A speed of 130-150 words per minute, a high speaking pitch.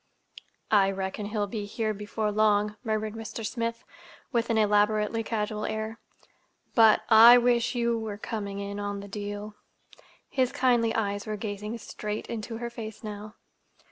Yes: average, 145 wpm; high, 215 Hz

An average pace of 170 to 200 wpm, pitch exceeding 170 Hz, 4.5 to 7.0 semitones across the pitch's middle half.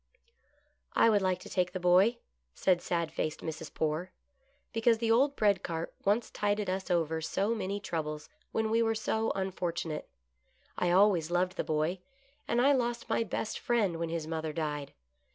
Yes: average, 180 wpm; medium, 185 Hz; average, 5.2 semitones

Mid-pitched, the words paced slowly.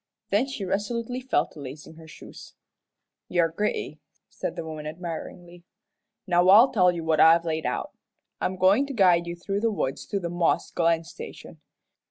No: medium, 175 Hz; average, 180 wpm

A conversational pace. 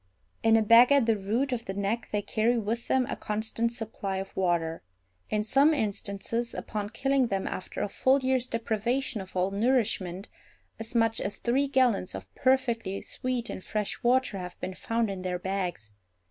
Yes: average, 180 wpm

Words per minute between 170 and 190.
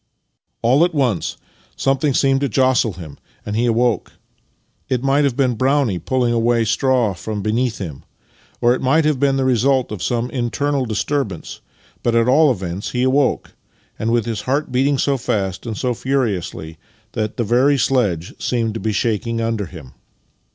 Yes: average, 175 wpm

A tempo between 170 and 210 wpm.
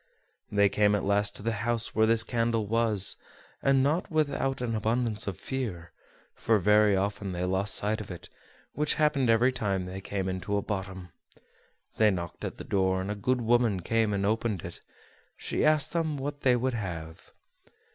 Yes: average, 180 wpm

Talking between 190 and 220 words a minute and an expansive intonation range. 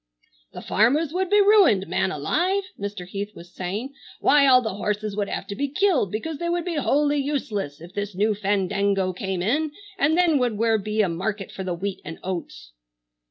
Yes: average, 200 wpm; wide, 7.2 semitones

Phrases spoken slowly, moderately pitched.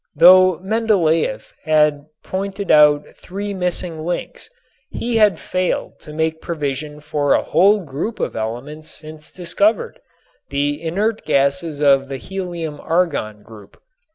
Yes: slow, 125 wpm; medium, 160 Hz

